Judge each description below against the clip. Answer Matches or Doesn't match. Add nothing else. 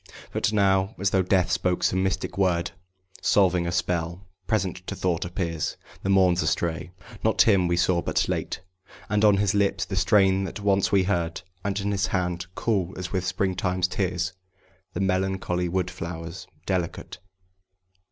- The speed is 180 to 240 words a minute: Doesn't match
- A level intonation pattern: Matches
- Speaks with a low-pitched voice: Matches